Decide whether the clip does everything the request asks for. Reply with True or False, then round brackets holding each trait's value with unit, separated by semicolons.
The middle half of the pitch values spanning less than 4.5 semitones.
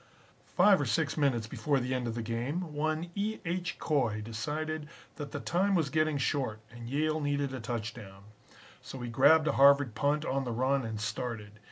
False (5.0 semitones)